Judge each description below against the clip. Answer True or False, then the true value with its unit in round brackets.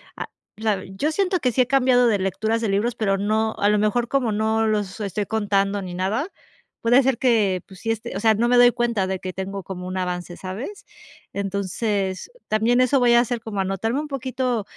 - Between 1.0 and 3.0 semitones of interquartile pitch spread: False (3.7 semitones)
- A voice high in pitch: True (220 Hz)